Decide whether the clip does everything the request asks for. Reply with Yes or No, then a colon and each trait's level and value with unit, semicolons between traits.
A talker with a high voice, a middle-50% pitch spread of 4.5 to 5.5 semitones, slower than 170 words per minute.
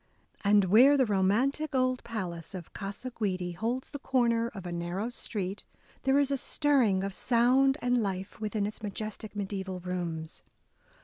Yes: high, 215 Hz; average, 4.9 semitones; average, 160 wpm